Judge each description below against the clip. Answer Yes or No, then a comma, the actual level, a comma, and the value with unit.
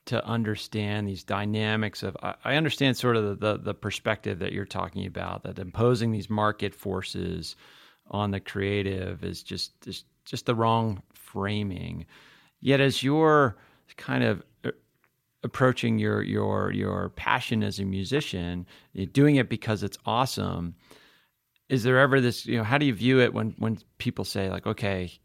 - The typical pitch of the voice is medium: No, low, 105 Hz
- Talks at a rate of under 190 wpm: Yes, average, 160 wpm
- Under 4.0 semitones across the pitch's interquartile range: Yes, average, 3.6 semitones